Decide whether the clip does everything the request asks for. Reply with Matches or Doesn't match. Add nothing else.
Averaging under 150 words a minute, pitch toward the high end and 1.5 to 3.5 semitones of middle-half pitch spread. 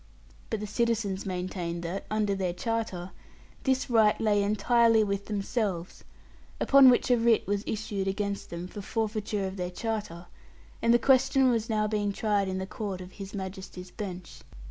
Doesn't match